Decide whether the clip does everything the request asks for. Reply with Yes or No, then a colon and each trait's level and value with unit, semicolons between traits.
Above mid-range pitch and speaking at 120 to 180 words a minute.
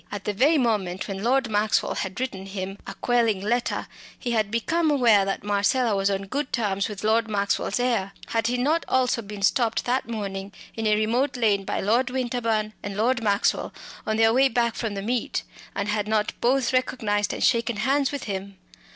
No: high, 220 Hz; average, 195 wpm